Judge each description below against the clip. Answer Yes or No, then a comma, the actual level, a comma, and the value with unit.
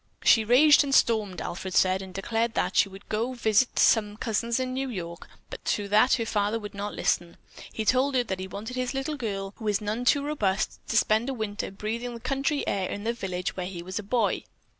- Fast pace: Yes, fast, 230 wpm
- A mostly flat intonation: No, average, 4.0 semitones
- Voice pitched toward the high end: Yes, high, 215 Hz